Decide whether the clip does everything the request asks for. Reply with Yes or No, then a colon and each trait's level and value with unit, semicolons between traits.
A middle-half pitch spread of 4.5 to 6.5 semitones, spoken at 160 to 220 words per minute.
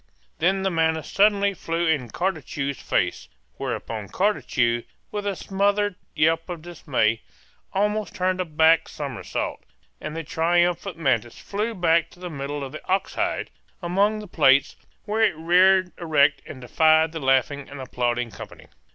No: average, 5.1 semitones; average, 150 wpm